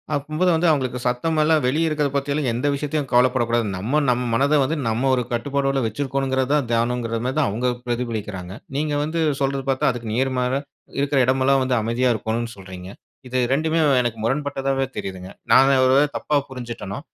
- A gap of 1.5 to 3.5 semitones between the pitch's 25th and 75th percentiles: Yes, average, 3.2 semitones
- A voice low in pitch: Yes, low, 130 Hz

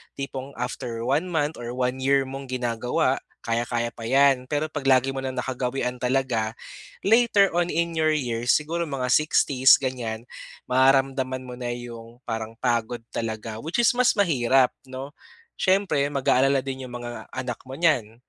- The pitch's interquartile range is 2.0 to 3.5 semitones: Yes, narrow, 2.6 semitones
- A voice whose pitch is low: Yes, low, 130 Hz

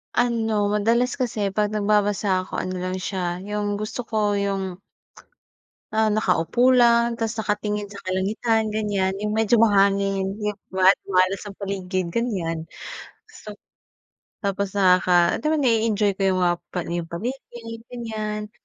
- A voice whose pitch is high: Yes, high, 205 Hz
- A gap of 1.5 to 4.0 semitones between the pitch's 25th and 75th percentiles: Yes, average, 2.7 semitones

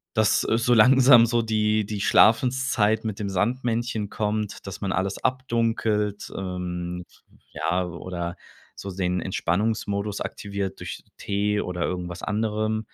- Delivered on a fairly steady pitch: No, average, 3.0 semitones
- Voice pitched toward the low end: Yes, low, 105 Hz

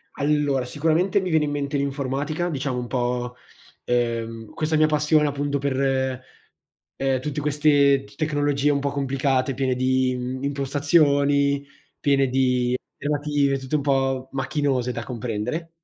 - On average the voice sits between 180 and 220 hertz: No, medium, 140 Hz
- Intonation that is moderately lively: No, narrow, 2.0 semitones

